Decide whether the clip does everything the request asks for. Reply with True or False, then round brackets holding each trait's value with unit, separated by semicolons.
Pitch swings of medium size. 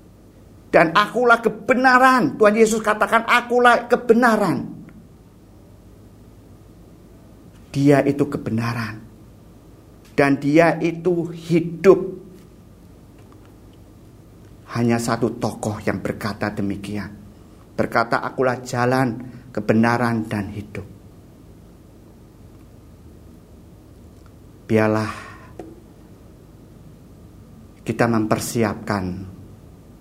False (5.7 semitones)